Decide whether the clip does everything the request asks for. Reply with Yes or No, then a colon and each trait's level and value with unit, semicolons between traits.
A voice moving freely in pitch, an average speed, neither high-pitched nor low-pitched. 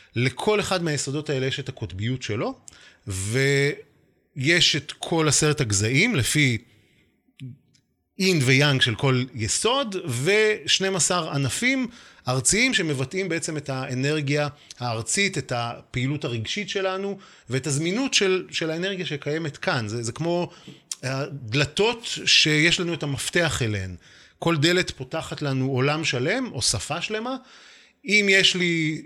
Yes: wide, 5.9 semitones; average, 120 wpm; medium, 150 Hz